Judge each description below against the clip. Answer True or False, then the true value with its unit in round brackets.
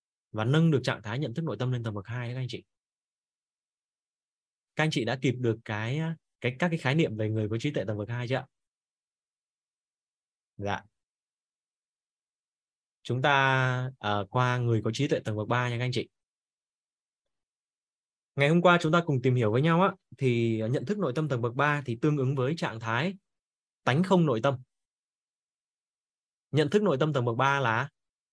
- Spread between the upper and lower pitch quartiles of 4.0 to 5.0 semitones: True (4.5 semitones)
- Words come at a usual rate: True (195 wpm)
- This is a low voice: True (130 Hz)